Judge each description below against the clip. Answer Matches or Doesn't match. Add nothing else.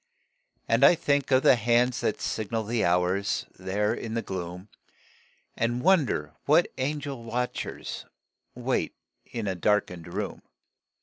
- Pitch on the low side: Matches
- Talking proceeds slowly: Matches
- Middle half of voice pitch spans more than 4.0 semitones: Matches